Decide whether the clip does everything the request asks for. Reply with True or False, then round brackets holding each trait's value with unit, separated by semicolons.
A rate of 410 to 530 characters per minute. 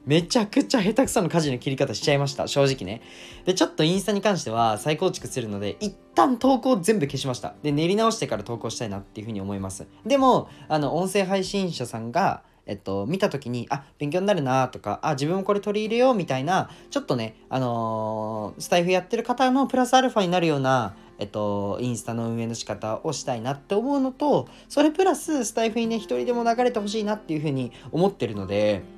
True (450 characters per minute)